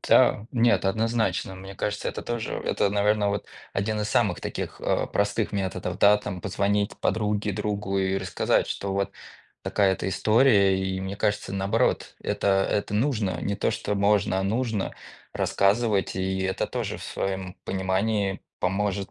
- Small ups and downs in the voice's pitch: Yes, narrow, 1.6 semitones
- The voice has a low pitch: Yes, low, 100 Hz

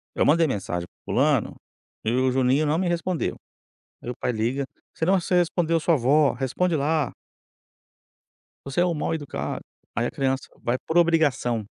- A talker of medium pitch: Yes, medium, 145 Hz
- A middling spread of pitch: Yes, average, 4.8 semitones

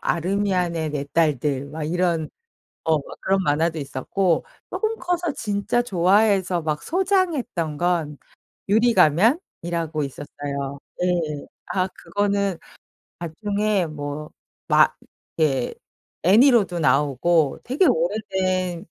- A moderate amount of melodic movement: Yes, average, 4.9 semitones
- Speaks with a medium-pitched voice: Yes, medium, 175 Hz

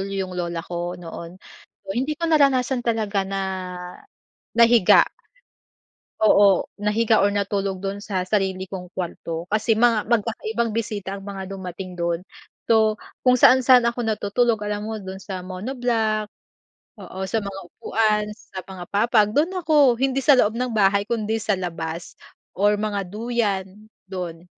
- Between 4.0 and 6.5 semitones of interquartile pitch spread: No, average, 3.4 semitones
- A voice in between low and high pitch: No, high, 205 Hz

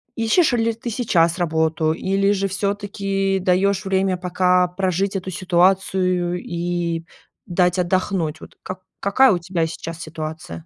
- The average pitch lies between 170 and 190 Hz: Yes, medium, 185 Hz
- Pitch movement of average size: No, narrow, 2.3 semitones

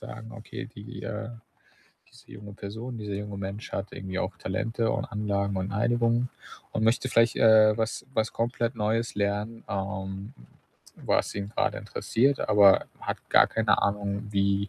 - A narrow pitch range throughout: Yes, narrow, 2.3 semitones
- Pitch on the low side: Yes, low, 105 Hz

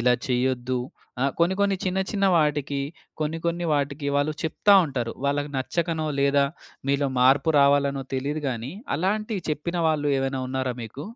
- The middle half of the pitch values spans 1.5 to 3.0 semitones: No, average, 3.4 semitones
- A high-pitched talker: No, medium, 145 Hz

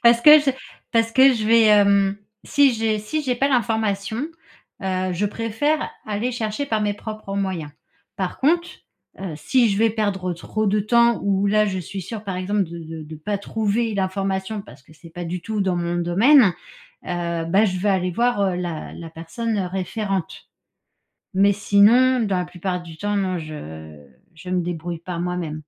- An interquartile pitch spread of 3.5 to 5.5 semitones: Yes, average, 3.8 semitones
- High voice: Yes, high, 200 Hz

